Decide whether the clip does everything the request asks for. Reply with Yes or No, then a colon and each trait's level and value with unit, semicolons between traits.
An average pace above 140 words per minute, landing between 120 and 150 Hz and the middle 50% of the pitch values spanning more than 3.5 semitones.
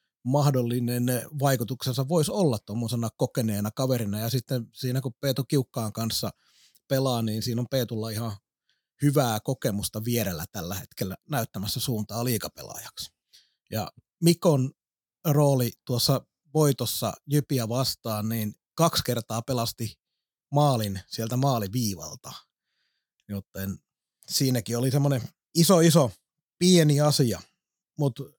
No: average, 110 wpm; low, 125 Hz; average, 3.9 semitones